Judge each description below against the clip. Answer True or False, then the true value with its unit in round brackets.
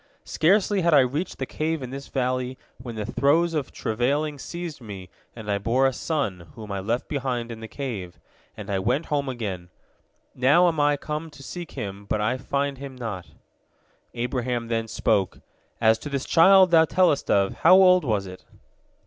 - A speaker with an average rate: True (185 wpm)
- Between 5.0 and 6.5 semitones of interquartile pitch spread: True (5.3 semitones)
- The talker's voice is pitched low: True (130 Hz)